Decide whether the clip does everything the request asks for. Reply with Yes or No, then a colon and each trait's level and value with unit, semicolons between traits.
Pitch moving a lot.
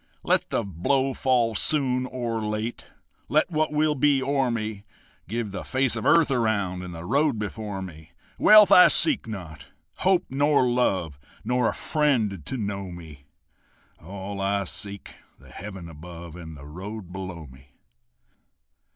Yes: wide, 6.5 semitones